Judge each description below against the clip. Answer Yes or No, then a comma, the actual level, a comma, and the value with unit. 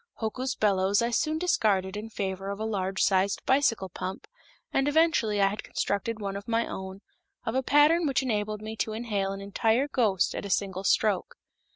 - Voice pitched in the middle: No, high, 210 Hz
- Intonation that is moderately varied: Yes, average, 3.5 semitones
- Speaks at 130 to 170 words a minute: No, average, 190 wpm